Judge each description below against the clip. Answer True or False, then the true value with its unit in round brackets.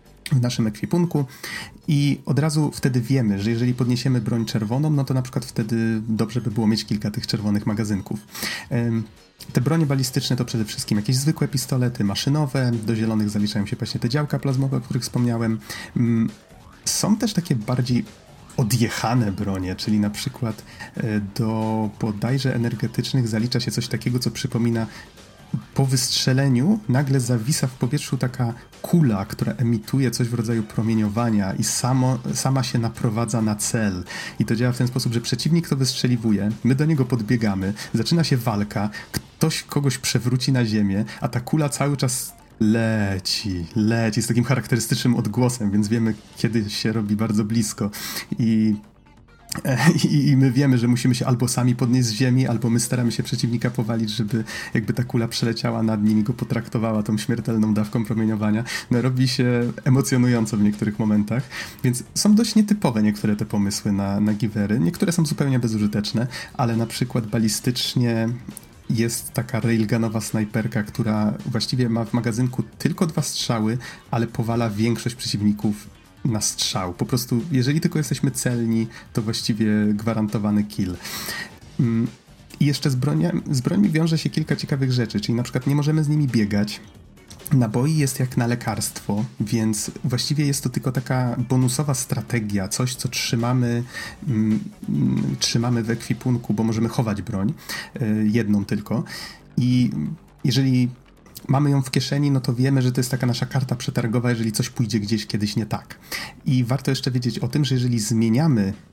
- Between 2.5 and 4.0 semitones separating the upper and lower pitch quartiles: True (3.0 semitones)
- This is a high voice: False (120 Hz)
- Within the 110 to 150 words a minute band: False (160 wpm)